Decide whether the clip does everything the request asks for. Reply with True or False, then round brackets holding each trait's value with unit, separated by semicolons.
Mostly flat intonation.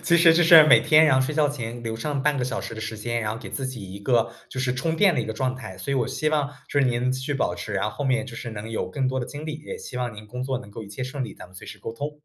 False (4.2 semitones)